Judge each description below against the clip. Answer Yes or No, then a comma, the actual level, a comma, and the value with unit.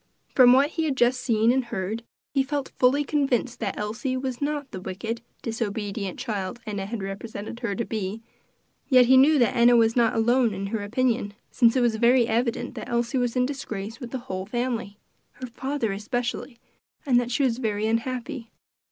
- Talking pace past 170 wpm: Yes, average, 190 wpm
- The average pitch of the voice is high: Yes, high, 235 Hz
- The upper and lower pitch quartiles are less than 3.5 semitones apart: Yes, average, 2.8 semitones